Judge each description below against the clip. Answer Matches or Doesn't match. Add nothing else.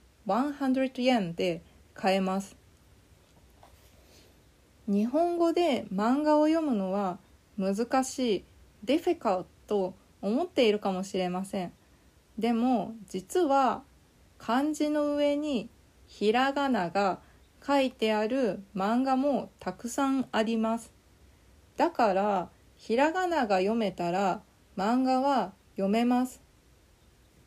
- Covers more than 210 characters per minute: Doesn't match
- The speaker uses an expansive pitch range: Matches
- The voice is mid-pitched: Doesn't match